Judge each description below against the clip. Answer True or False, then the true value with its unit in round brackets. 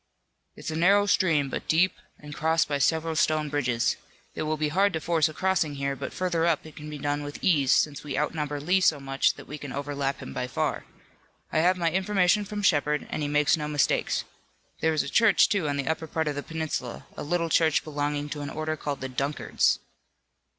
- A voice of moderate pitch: True (150 Hz)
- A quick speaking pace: True (220 wpm)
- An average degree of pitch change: False (2.3 semitones)